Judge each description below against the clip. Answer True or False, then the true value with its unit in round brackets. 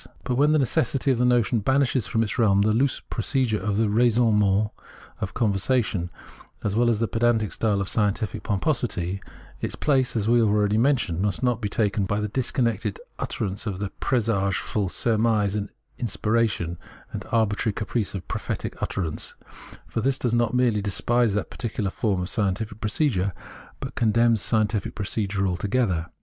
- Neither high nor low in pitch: False (110 Hz)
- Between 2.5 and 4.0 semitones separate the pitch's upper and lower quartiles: True (3.0 semitones)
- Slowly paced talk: False (170 wpm)